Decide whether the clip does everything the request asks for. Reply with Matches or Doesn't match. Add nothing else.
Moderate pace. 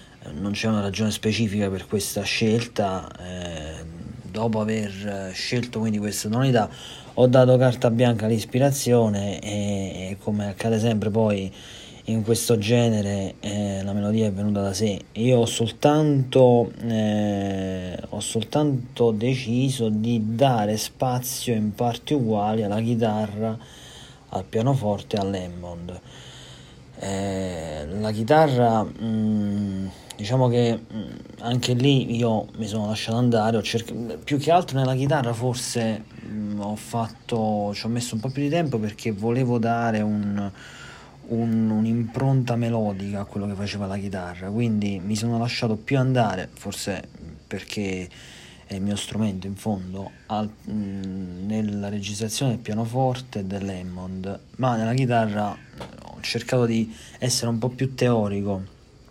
Matches